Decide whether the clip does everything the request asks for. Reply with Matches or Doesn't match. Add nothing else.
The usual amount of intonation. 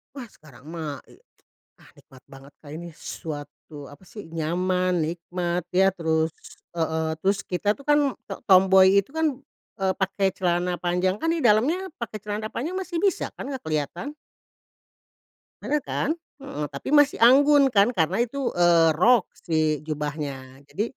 Doesn't match